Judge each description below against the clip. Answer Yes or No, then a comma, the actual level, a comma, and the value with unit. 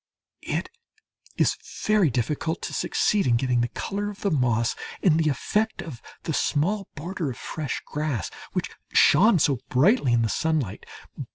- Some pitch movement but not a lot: No, wide, 7.3 semitones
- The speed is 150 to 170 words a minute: Yes, average, 160 wpm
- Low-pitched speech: No, medium, 155 Hz